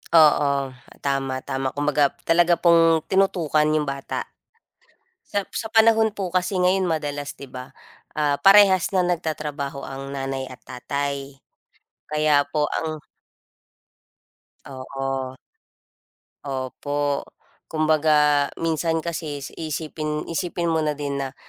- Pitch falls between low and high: Yes, medium, 150 Hz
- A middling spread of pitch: Yes, average, 3.1 semitones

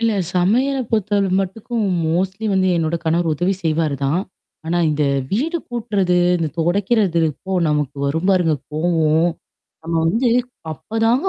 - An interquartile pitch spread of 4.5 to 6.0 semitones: Yes, average, 5.0 semitones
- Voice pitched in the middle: Yes, medium, 180 Hz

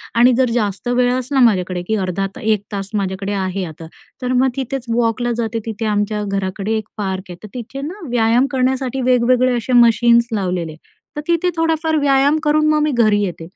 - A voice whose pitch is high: Yes, high, 235 Hz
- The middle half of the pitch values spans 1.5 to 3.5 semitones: No, average, 4.3 semitones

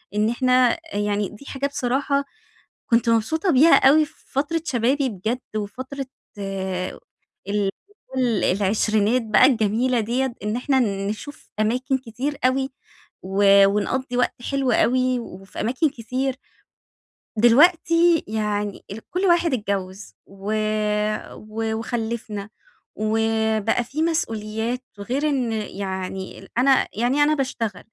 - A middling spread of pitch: Yes, average, 4.2 semitones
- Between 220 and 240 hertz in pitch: Yes, high, 235 Hz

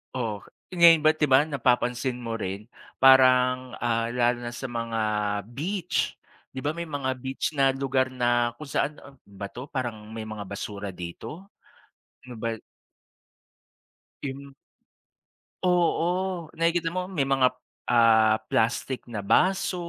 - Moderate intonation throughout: Yes, average, 4.5 semitones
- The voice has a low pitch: Yes, low, 130 Hz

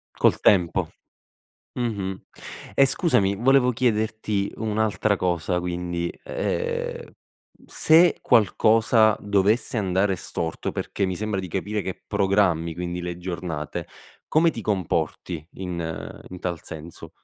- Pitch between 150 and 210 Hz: No, low, 100 Hz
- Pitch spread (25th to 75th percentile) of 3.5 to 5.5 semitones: Yes, average, 3.9 semitones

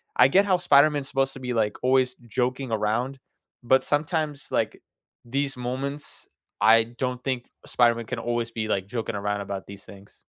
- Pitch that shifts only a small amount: No, average, 3.2 semitones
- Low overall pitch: Yes, low, 125 Hz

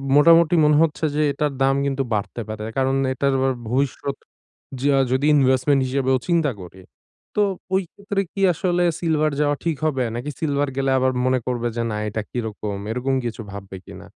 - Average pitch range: Yes, average, 3.1 semitones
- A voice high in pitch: No, low, 135 Hz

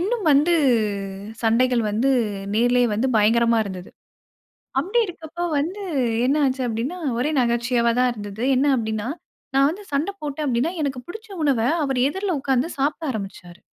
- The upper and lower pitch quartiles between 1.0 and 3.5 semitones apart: No, average, 4.7 semitones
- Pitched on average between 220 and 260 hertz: Yes, very high, 255 Hz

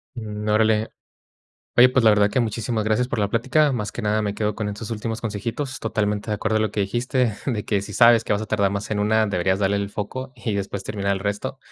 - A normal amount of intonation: No, narrow, 2.2 semitones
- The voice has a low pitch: Yes, low, 105 Hz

